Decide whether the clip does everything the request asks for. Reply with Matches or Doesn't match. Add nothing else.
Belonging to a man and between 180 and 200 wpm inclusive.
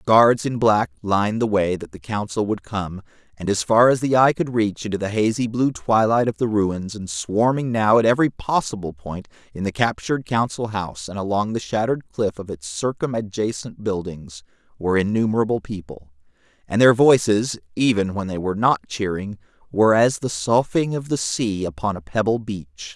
Matches